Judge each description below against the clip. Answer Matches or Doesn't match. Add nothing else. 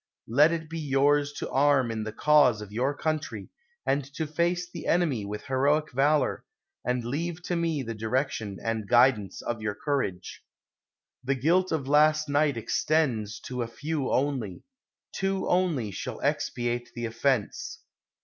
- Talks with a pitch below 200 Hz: Matches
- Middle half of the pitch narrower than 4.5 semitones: Doesn't match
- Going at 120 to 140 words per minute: Doesn't match